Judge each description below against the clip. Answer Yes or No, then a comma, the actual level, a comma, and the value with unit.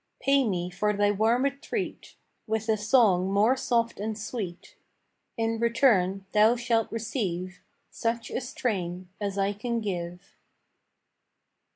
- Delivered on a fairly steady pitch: No, average, 3.2 semitones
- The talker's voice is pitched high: Yes, high, 215 Hz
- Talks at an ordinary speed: No, slow, 130 wpm